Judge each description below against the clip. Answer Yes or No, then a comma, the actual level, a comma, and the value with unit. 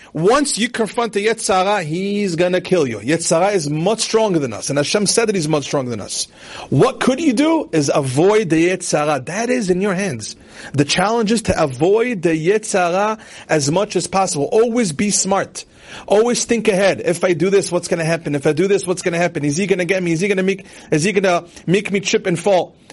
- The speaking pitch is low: No, high, 190 Hz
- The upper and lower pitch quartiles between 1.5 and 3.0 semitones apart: No, average, 4.2 semitones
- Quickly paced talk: Yes, fast, 220 wpm